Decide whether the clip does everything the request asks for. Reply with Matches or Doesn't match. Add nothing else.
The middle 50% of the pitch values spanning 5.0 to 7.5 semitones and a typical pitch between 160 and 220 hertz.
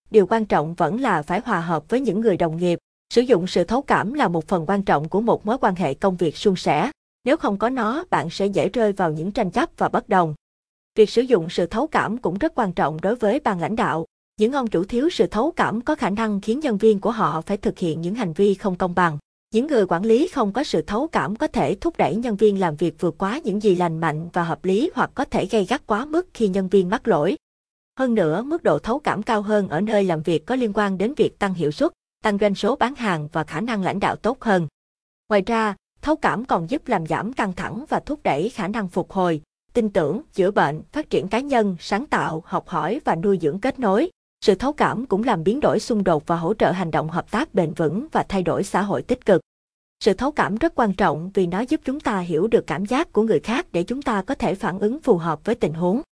Doesn't match